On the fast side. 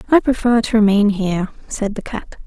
No: average, 195 wpm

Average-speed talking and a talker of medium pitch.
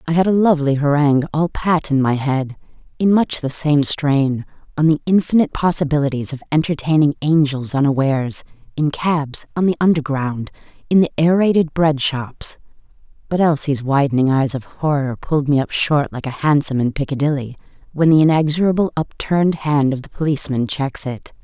Yes: average, 160 wpm; medium, 150 Hz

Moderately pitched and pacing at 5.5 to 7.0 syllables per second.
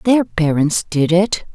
No: medium, 175 Hz; 3.7 syllables/s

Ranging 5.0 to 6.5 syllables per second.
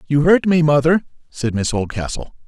Yes: 5.2 syllables/s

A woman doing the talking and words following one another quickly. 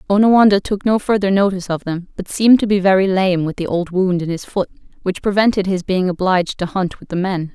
Yes: female; fast, 240 wpm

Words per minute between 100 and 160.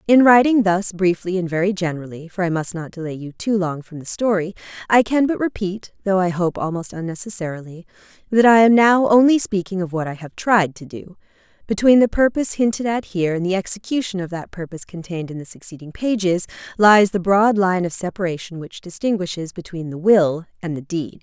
No: average, 195 wpm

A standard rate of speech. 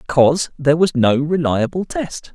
Yes: average, 155 wpm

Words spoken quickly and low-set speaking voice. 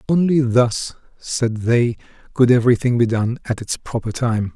No: average, 160 wpm; low, 120 Hz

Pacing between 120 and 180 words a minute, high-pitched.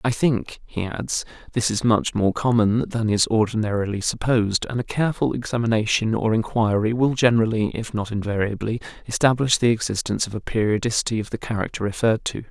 No: average, 170 wpm; low, 110 Hz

